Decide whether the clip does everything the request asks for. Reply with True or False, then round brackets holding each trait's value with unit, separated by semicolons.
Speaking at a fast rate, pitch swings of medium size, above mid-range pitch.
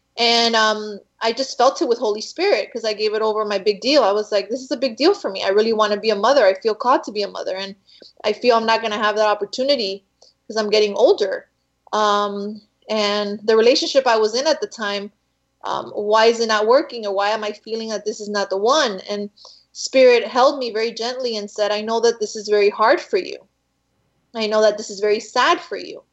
True (250 wpm; 3.0 semitones; 220 Hz)